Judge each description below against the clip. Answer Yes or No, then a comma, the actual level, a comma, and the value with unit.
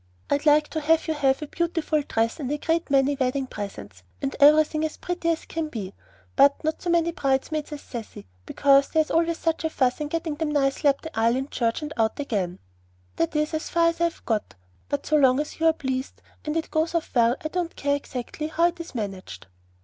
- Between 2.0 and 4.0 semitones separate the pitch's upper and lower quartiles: Yes, average, 3.6 semitones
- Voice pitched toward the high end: Yes, very high, 295 Hz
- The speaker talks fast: Yes, fast, 225 wpm